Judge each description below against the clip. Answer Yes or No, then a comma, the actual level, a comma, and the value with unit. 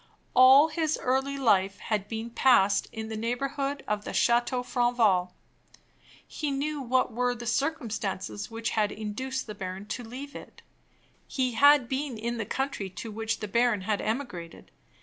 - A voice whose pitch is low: No, high, 235 Hz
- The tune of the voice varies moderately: Yes, average, 3.9 semitones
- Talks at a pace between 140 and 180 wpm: Yes, average, 160 wpm